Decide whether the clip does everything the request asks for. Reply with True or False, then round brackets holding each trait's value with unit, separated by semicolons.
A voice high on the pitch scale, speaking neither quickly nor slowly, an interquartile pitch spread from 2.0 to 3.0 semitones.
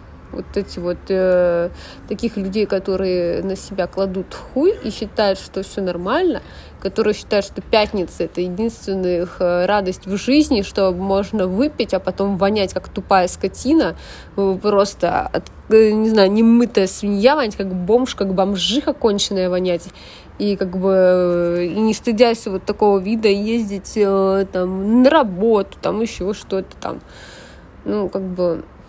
True (195 Hz; 140 wpm; 2.7 semitones)